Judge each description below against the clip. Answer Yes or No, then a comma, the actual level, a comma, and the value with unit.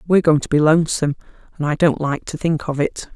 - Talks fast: Yes, fast, 230 wpm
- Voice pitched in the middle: Yes, medium, 155 Hz